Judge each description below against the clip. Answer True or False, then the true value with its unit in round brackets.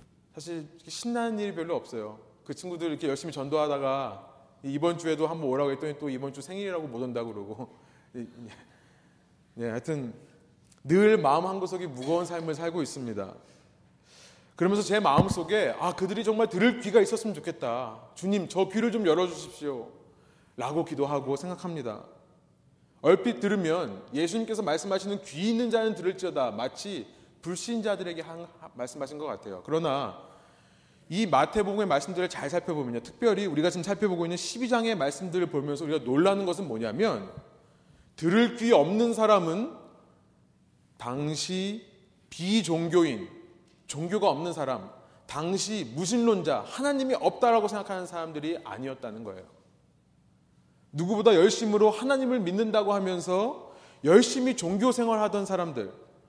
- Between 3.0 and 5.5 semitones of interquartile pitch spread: False (6.2 semitones)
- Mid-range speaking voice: True (175 Hz)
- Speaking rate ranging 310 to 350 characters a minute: True (325 characters per minute)